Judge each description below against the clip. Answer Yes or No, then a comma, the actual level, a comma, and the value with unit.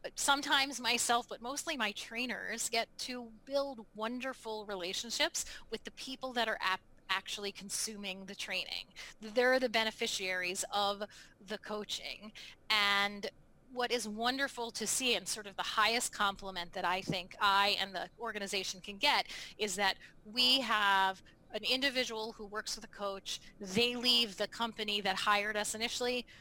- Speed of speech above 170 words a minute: No, average, 150 wpm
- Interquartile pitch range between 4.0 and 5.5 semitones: No, average, 3.3 semitones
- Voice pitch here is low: No, high, 215 Hz